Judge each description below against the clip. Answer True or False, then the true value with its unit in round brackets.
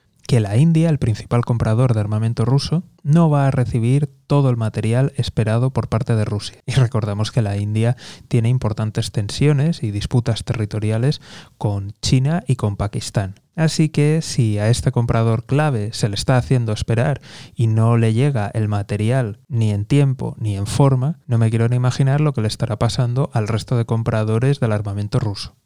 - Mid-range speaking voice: False (120 Hz)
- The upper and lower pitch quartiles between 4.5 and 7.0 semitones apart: False (3.7 semitones)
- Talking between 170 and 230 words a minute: True (180 wpm)